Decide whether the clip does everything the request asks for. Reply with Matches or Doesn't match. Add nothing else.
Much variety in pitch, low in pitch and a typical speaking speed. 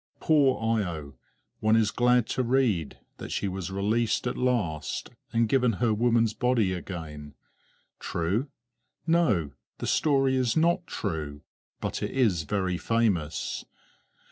Doesn't match